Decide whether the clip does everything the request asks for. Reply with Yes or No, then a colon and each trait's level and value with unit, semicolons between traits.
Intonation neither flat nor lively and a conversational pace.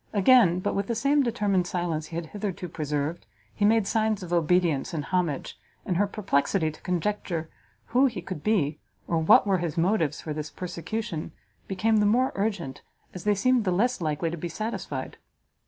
Yes: average, 4.4 semitones; average, 185 wpm